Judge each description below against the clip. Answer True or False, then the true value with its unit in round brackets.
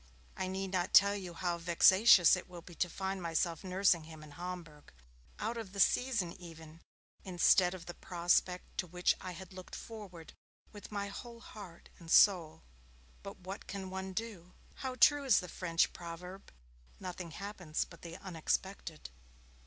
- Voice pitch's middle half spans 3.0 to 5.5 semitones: False (2.6 semitones)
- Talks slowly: False (165 wpm)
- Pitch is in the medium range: True (180 Hz)